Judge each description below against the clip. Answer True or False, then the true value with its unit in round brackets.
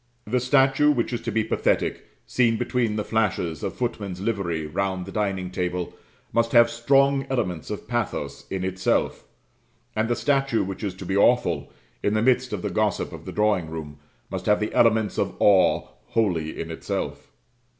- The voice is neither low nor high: False (105 Hz)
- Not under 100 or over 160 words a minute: False (180 wpm)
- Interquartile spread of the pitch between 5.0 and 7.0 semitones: False (4.3 semitones)